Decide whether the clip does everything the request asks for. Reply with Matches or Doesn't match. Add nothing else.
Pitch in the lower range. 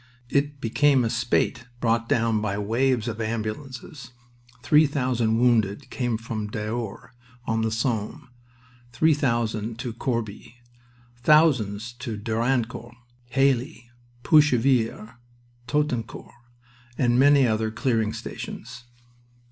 Matches